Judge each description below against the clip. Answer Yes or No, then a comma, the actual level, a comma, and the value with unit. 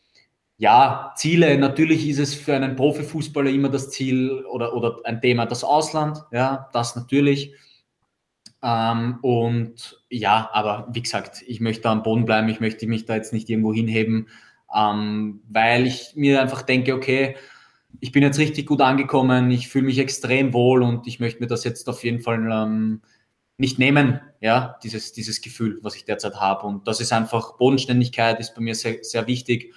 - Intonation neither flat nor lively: Yes, average, 3.0 semitones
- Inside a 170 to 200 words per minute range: Yes, average, 175 wpm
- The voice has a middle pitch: No, low, 120 Hz